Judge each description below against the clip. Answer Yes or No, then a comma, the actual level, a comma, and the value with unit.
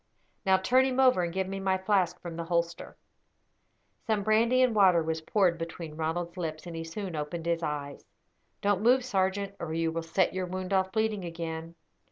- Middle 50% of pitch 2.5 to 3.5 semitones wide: Yes, average, 3.2 semitones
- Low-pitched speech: No, medium, 180 Hz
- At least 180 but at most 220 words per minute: Yes, average, 195 wpm